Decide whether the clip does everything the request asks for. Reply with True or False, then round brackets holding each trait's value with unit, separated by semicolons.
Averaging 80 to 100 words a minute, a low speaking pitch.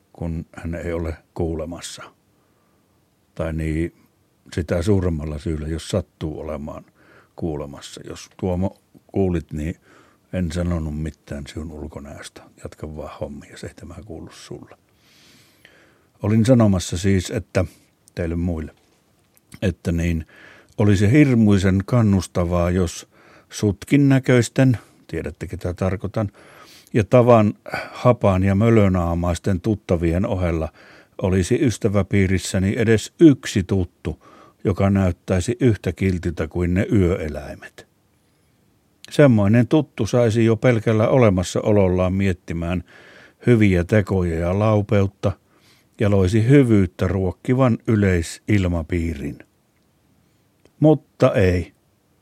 True (95 wpm; 95 Hz)